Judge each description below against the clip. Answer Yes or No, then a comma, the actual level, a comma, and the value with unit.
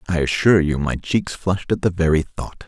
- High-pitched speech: No, very low, 85 Hz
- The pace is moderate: No, fast, 225 wpm